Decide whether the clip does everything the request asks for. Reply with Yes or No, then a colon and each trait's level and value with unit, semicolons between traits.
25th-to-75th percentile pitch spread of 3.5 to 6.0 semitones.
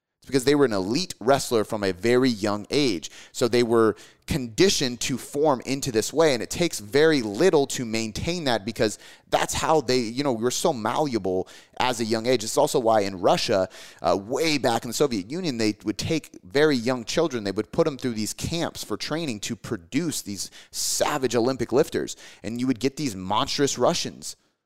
Yes: average, 4.4 semitones